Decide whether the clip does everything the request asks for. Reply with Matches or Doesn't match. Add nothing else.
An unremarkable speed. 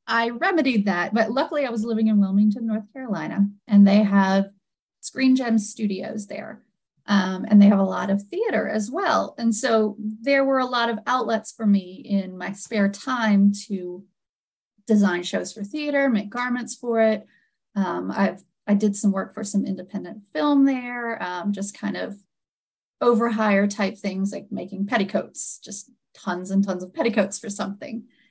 Matches